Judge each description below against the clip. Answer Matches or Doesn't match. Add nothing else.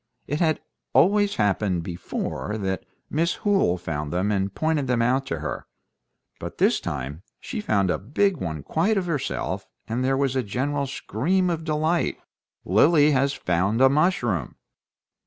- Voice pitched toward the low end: Matches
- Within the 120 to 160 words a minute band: Matches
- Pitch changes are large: Matches